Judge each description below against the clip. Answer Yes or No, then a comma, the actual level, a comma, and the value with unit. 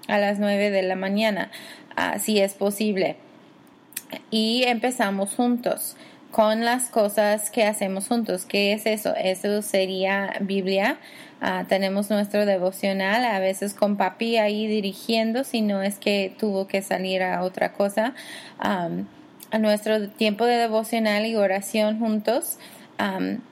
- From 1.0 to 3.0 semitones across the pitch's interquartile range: Yes, average, 2.7 semitones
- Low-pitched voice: No, high, 215 Hz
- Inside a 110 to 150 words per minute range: Yes, average, 140 wpm